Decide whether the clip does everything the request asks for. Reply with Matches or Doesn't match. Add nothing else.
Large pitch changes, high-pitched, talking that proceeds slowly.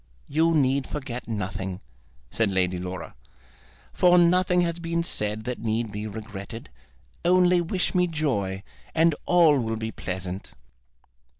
Doesn't match